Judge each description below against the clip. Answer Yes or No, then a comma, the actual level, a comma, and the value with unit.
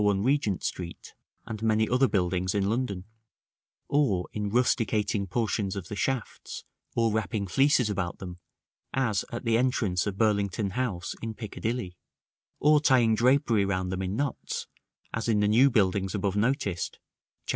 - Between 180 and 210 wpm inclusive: No, average, 155 wpm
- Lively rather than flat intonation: No, average, 3.8 semitones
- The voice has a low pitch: Yes, low, 105 Hz